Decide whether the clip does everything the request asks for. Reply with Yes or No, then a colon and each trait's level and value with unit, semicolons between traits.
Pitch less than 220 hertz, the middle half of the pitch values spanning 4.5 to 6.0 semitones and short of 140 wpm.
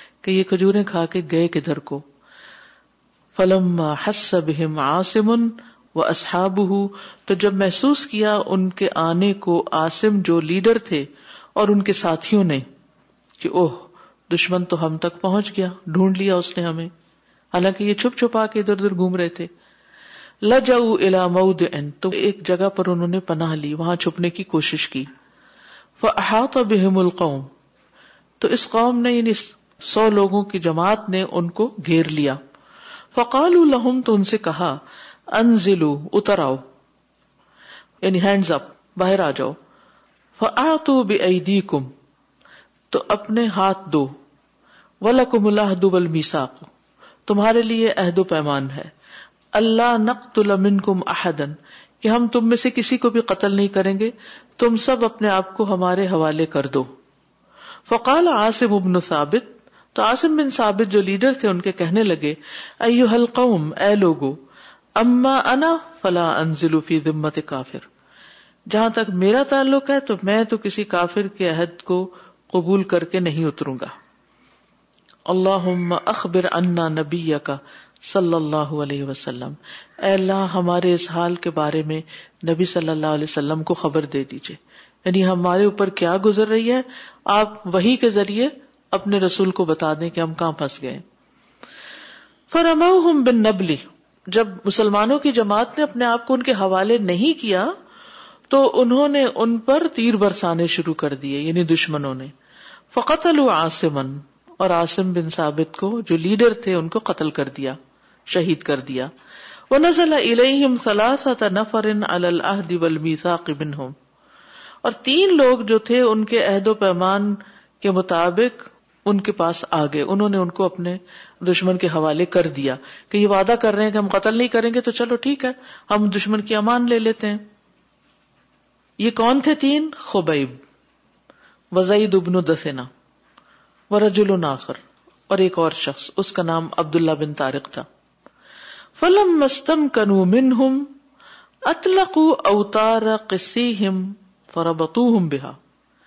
No: high, 195 Hz; average, 5.2 semitones; average, 145 wpm